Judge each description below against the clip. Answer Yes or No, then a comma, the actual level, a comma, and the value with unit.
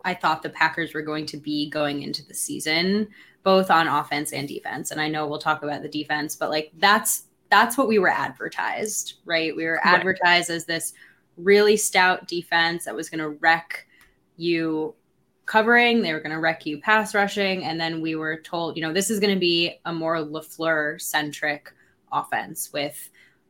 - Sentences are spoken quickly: No, average, 190 wpm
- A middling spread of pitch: Yes, average, 3.0 semitones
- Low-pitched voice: No, medium, 165 Hz